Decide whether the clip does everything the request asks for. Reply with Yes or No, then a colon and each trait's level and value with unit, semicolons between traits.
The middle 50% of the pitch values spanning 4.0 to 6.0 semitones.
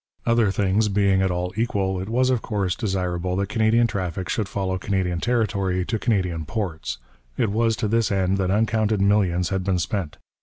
No: average, 3.0 semitones